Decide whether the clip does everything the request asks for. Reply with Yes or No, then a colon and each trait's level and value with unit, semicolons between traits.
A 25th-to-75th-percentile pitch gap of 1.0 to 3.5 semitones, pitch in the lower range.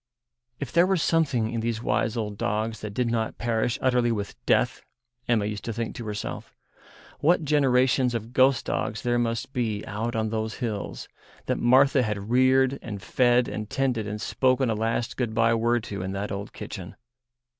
Yes: average, 2.8 semitones; low, 115 Hz